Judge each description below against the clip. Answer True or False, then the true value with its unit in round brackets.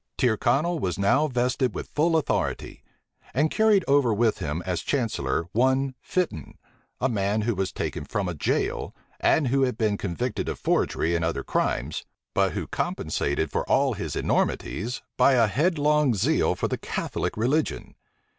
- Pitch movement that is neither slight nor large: False (6.4 semitones)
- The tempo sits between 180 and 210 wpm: False (160 wpm)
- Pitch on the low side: True (120 Hz)